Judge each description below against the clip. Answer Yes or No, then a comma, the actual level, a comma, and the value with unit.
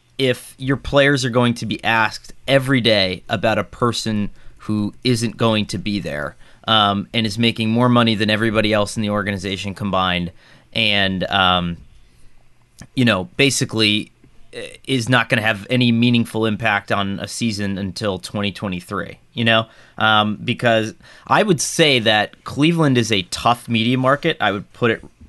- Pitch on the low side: Yes, low, 110 Hz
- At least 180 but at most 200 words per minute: No, average, 160 wpm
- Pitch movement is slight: No, average, 3.0 semitones